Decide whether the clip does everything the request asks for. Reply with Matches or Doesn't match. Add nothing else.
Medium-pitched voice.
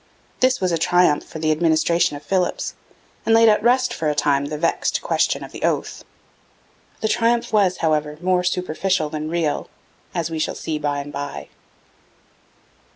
Matches